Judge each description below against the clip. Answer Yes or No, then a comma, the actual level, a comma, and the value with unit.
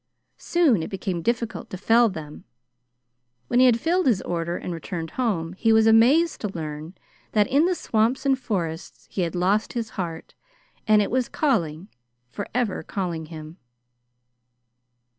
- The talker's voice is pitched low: No, high, 205 Hz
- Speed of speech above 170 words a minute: No, average, 155 wpm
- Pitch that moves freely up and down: Yes, wide, 6.0 semitones